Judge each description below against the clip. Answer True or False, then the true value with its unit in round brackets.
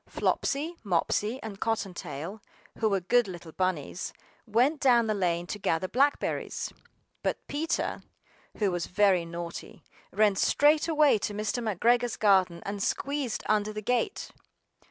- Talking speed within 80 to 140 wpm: True (135 wpm)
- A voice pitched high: True (210 Hz)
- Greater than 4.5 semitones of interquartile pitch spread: True (4.9 semitones)